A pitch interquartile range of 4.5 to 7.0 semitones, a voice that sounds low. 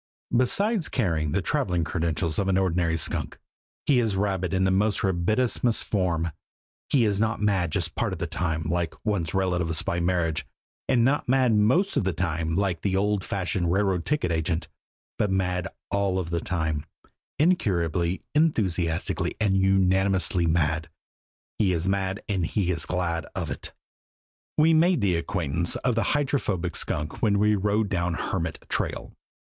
No: average, 3.7 semitones; very low, 95 Hz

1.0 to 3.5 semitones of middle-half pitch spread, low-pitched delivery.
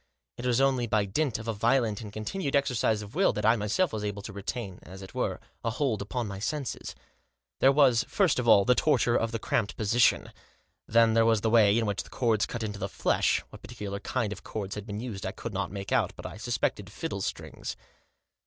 Yes: average, 3.2 semitones; low, 110 Hz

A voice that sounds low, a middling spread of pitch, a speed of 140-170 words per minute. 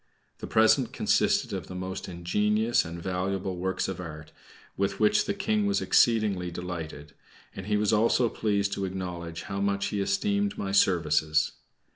Yes: very low, 95 Hz; average, 3.4 semitones; average, 160 wpm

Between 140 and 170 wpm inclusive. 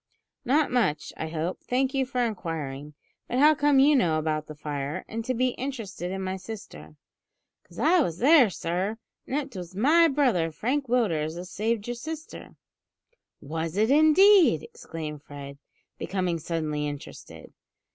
Yes: average, 165 wpm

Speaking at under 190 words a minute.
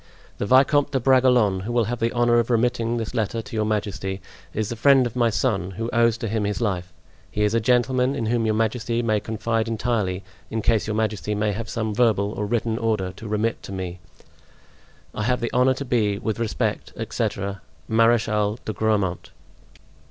No: average, 195 wpm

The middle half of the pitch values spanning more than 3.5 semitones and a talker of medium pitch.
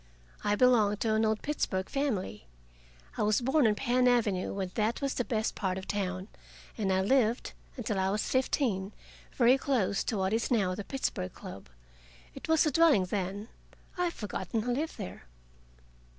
No: average, 4.7 semitones; high, 215 Hz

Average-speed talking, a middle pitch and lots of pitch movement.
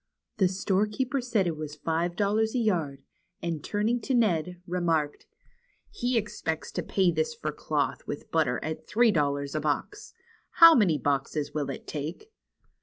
Yes: average, 165 wpm; medium, 180 Hz; wide, 6.4 semitones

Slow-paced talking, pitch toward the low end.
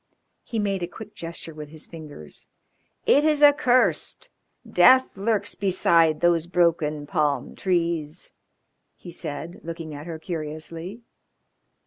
No: slow, 120 wpm; medium, 170 Hz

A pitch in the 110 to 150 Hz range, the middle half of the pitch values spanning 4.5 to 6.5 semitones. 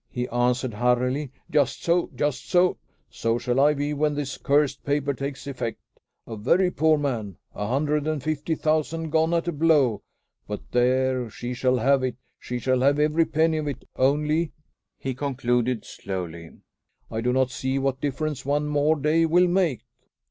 No: medium, 140 Hz; average, 3.6 semitones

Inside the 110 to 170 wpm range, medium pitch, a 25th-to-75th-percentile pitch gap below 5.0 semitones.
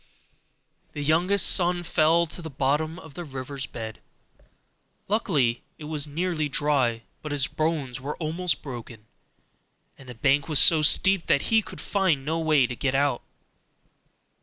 Yes: average, 155 wpm; medium, 150 Hz; average, 3.7 semitones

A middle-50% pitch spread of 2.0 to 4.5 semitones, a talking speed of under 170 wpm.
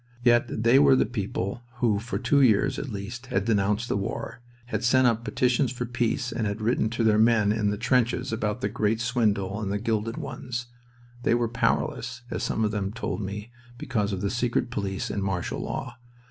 No: average, 2.9 semitones; average, 200 wpm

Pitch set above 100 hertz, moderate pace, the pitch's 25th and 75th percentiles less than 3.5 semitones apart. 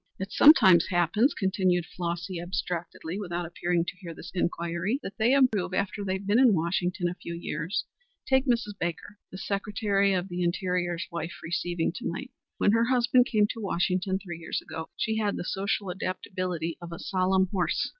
Yes: medium, 185 Hz; average, 175 wpm; average, 3.0 semitones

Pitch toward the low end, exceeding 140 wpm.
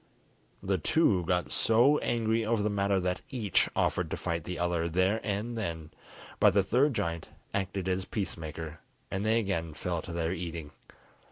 Yes: very low, 95 Hz; average, 175 wpm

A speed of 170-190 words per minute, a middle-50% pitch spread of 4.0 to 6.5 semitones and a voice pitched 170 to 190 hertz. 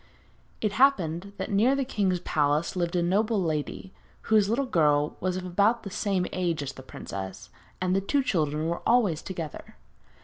Yes: average, 175 wpm; average, 4.7 semitones; medium, 185 Hz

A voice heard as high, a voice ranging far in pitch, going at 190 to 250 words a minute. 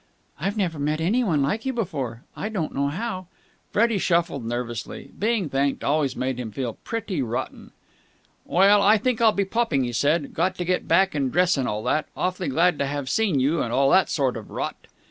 No: medium, 160 Hz; wide, 6.4 semitones; fast, 205 wpm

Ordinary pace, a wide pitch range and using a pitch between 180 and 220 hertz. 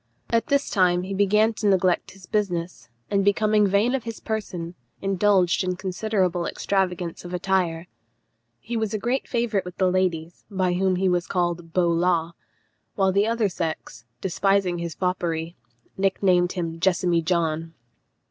No: average, 155 wpm; narrow, 2.5 semitones; medium, 185 Hz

